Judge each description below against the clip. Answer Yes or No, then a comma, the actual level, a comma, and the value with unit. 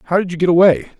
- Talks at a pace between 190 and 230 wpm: No, fast, 300 wpm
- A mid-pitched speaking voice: Yes, medium, 175 Hz